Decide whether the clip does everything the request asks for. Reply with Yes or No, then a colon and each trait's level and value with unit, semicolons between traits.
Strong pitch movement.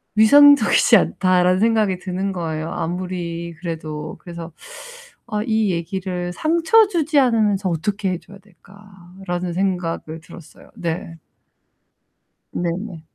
No: average, 3.5 semitones